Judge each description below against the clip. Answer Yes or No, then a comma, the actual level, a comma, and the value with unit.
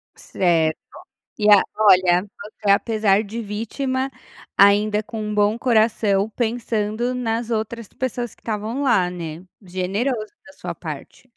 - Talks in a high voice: Yes, high, 215 Hz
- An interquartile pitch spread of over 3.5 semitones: No, average, 2.8 semitones